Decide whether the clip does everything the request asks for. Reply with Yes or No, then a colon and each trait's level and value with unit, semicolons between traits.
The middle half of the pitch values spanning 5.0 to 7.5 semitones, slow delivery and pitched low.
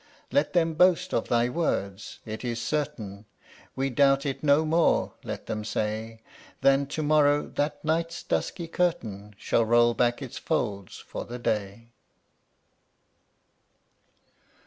Yes: wide, 5.6 semitones; slow, 130 wpm; low, 130 Hz